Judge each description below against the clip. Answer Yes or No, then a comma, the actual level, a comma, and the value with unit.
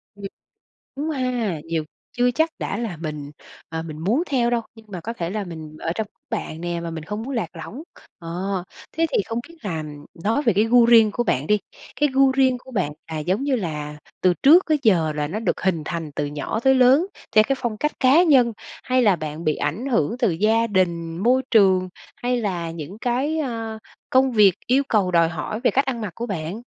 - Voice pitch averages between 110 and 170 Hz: No, high, 215 Hz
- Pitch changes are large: Yes, wide, 6.8 semitones